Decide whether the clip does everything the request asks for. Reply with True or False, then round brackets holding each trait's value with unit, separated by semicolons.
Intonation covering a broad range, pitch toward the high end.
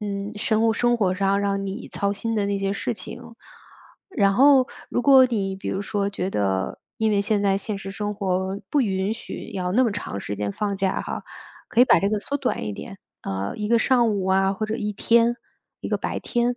False (2.7 semitones; 200 Hz)